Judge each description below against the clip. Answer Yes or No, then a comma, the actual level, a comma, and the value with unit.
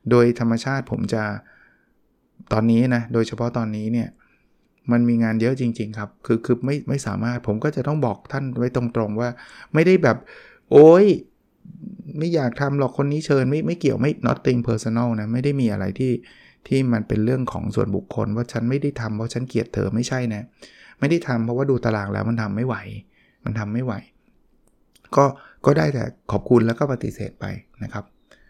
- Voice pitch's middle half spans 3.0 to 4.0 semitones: Yes, average, 3.3 semitones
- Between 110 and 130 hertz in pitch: Yes, low, 120 Hz